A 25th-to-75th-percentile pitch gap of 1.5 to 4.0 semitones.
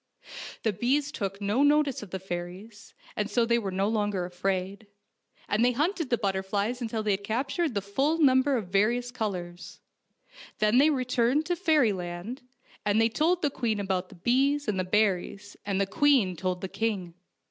No: average, 5.1 semitones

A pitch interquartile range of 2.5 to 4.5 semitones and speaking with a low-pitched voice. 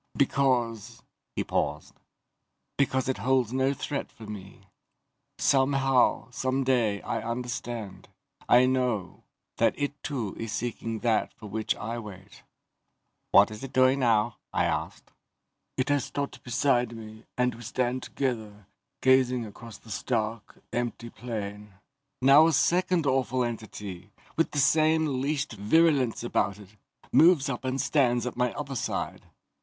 Yes: average, 3.4 semitones; low, 125 Hz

